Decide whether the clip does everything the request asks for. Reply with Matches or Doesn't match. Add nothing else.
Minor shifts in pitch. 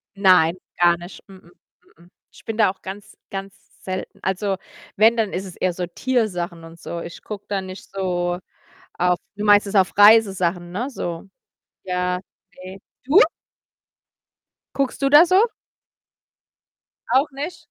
Doesn't match